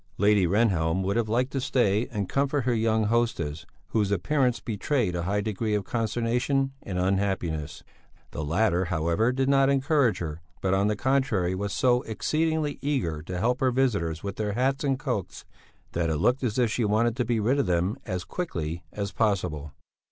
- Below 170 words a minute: No, average, 185 wpm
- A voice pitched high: No, low, 105 Hz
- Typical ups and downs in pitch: No, wide, 5.7 semitones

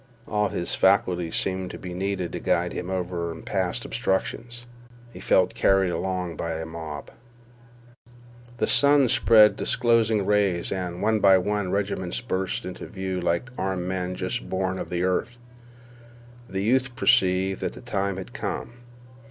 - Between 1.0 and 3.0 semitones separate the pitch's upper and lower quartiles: Yes, average, 2.7 semitones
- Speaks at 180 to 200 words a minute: No, average, 155 wpm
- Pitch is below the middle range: Yes, very low, 95 Hz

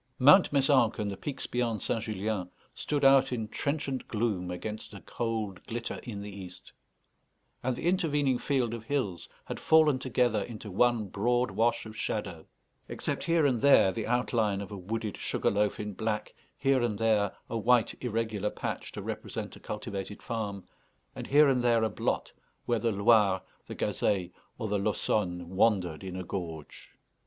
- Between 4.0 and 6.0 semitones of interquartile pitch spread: No, average, 3.5 semitones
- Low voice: Yes, low, 110 Hz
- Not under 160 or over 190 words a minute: Yes, average, 170 wpm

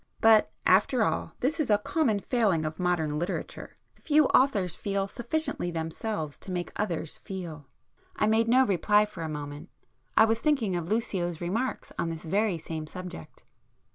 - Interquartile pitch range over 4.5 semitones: Yes, average, 5.2 semitones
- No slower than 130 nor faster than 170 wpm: Yes, average, 165 wpm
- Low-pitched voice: No, high, 195 Hz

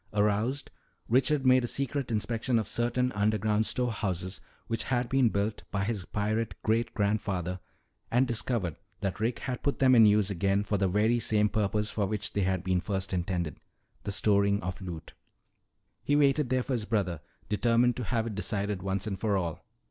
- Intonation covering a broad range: No, average, 3.4 semitones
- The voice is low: Yes, low, 105 Hz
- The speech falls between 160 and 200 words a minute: Yes, average, 180 wpm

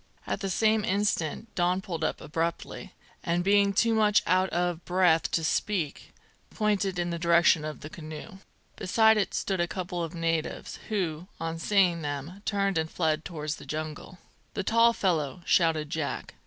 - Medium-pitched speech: Yes, medium, 175 Hz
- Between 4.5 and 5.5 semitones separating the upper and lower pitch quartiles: No, average, 3.6 semitones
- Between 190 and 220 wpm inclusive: No, average, 170 wpm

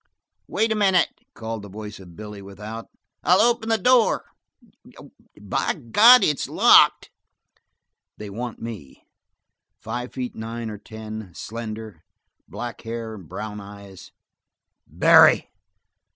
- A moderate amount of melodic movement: Yes, average, 3.1 semitones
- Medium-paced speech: No, slow, 125 wpm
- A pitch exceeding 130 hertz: No, low, 110 Hz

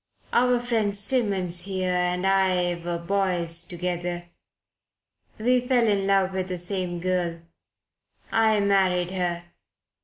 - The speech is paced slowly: Yes, slow, 120 wpm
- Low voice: No, medium, 185 Hz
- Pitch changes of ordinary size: No, narrow, 2.2 semitones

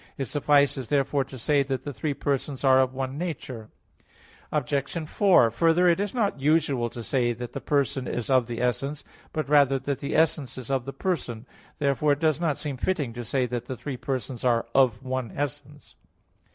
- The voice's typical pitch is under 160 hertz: Yes, low, 135 Hz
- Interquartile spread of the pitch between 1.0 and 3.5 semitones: Yes, average, 2.7 semitones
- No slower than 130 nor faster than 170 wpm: No, average, 195 wpm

